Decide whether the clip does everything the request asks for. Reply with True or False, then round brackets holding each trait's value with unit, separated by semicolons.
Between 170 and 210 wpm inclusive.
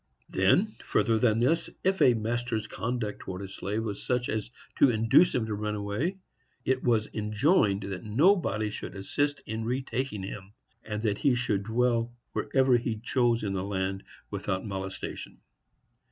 False (160 wpm)